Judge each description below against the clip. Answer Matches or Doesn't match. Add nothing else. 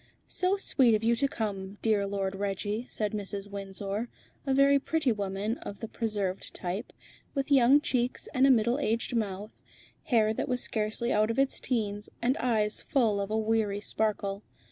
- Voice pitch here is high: Matches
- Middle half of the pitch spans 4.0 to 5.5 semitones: Doesn't match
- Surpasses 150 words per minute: Matches